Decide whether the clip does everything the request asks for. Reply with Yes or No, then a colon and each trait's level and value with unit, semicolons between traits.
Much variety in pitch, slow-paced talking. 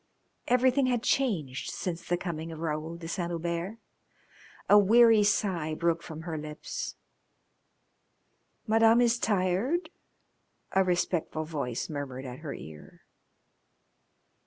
Yes: wide, 5.7 semitones; slow, 115 wpm